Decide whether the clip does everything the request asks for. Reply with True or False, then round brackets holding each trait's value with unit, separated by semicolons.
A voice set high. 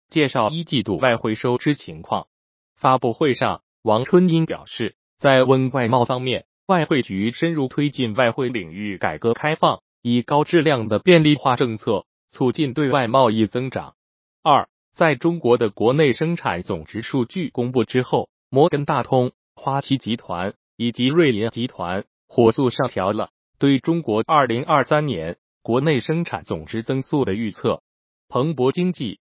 False (130 Hz)